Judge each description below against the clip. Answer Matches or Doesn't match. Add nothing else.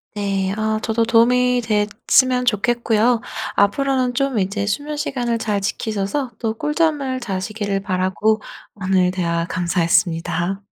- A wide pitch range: Doesn't match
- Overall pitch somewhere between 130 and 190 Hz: Doesn't match